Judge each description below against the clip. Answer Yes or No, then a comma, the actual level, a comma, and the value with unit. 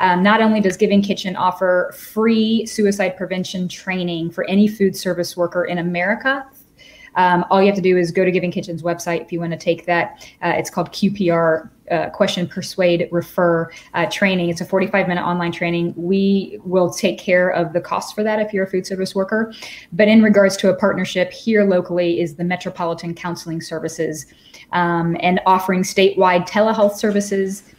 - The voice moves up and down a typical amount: No, narrow, 2.3 semitones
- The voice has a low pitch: No, medium, 185 Hz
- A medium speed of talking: Yes, average, 185 wpm